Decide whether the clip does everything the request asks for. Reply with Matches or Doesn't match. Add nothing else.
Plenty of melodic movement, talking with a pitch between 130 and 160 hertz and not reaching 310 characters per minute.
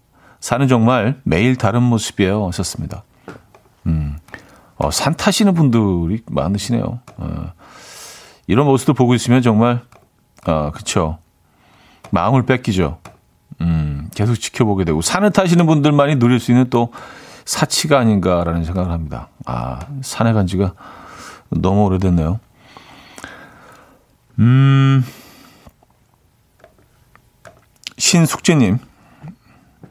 Doesn't match